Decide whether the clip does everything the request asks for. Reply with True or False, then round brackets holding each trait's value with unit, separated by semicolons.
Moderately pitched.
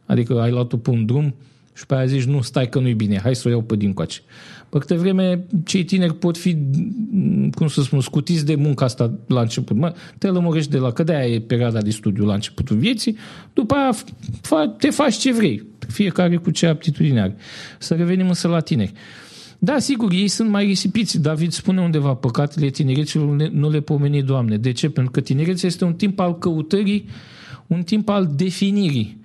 True (160 Hz)